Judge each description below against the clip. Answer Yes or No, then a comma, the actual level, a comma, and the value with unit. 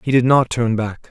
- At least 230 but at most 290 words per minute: Yes, fast, 270 wpm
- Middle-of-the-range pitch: No, low, 120 Hz